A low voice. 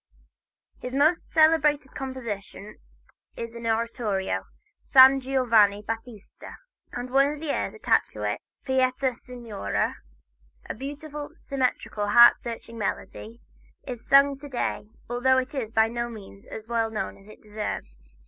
No: high, 240 Hz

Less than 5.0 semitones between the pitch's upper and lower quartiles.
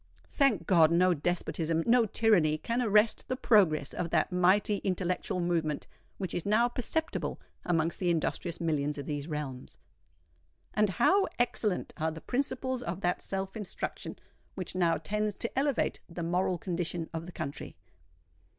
Yes: average, 4.5 semitones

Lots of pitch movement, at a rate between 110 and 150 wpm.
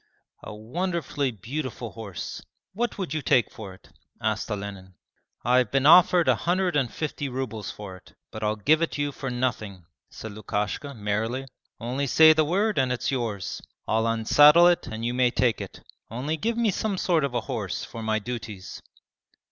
No: wide, 6.1 semitones; average, 180 wpm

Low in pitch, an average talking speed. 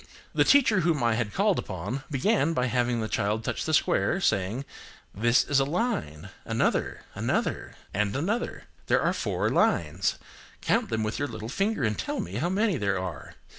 Yes: low, 125 Hz; average, 170 wpm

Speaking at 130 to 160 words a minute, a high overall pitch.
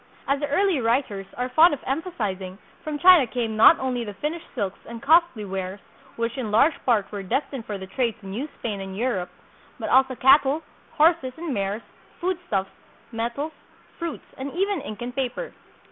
No: average, 175 wpm; very high, 250 Hz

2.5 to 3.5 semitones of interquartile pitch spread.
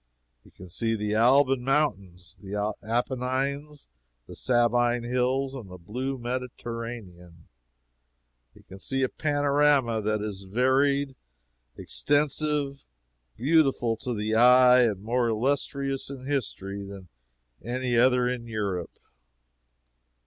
No: average, 4.1 semitones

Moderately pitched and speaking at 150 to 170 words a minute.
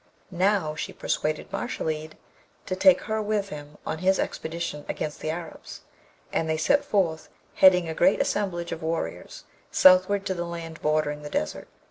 Yes: medium, 170 Hz; average, 160 wpm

